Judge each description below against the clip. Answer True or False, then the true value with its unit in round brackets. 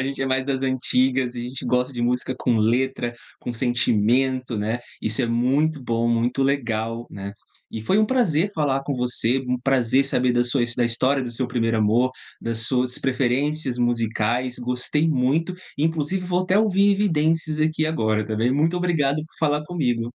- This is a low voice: True (130 Hz)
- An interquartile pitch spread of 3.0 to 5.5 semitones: True (3.8 semitones)